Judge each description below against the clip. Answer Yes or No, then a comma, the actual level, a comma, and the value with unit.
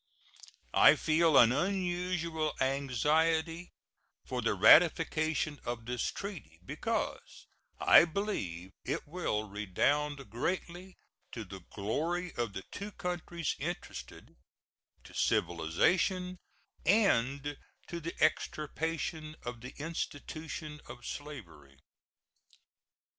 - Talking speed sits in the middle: No, slow, 95 wpm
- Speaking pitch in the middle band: Yes, medium, 155 Hz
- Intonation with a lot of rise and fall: Yes, wide, 6.1 semitones